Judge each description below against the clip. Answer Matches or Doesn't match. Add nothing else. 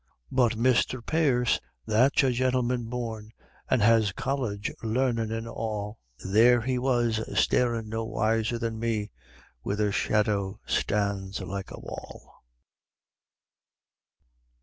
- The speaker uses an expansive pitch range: Doesn't match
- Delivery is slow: Matches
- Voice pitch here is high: Doesn't match